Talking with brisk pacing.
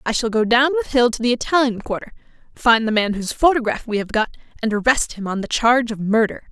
Yes: fast, 240 wpm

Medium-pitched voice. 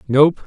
Yes: medium, 145 Hz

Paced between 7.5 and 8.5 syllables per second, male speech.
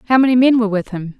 No: 8.1 syllables/s; female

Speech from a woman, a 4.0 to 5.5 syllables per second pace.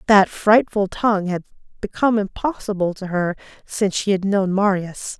Yes: female; 5.0 syllables/s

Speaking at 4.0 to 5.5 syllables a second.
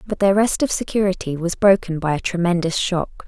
Yes: 5.4 syllables/s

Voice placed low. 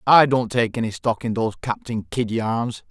Yes: low, 115 Hz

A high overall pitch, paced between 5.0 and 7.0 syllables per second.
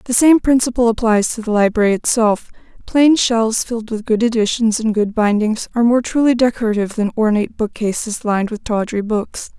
Yes: high, 225 Hz; 5.7 syllables/s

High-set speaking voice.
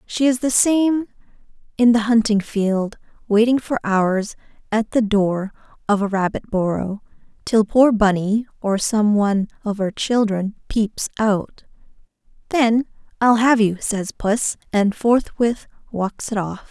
Yes: high, 215 Hz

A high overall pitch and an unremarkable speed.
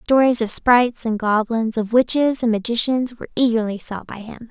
Yes: high, 230 Hz; average, 185 wpm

